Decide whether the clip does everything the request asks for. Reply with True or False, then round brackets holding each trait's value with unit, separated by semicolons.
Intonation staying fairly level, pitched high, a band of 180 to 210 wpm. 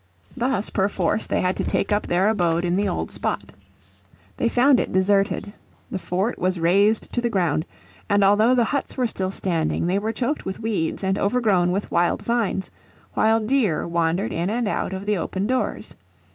False (3.7 semitones; 200 Hz; 185 wpm)